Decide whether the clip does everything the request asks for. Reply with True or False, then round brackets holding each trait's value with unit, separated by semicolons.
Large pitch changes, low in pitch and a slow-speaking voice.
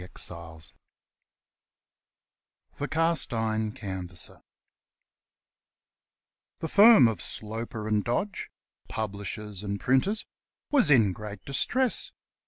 True (6.6 semitones; 110 Hz; 85 wpm)